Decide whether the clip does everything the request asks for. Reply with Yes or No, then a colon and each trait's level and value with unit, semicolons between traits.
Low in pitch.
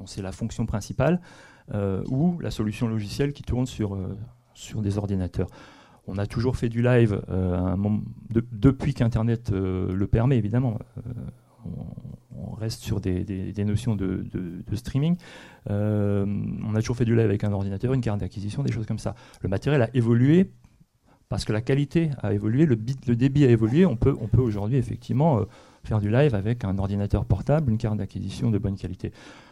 Yes: low, 110 Hz